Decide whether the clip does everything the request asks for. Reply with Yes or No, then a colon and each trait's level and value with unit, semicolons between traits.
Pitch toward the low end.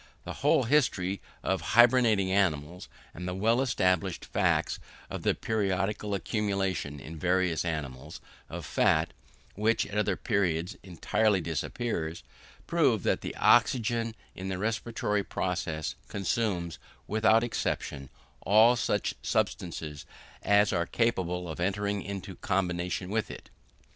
Yes: very low, 95 Hz